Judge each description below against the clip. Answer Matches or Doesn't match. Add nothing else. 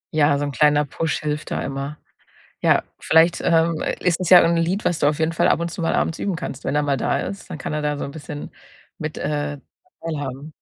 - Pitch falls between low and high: Matches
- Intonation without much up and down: Matches